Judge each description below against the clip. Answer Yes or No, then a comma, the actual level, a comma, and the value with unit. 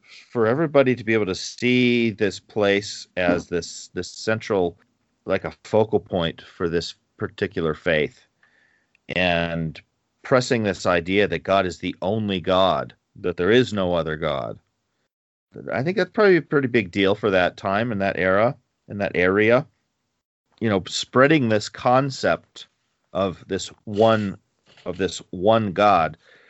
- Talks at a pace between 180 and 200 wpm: No, average, 150 wpm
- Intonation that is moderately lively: Yes, average, 4.2 semitones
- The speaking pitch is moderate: No, low, 105 Hz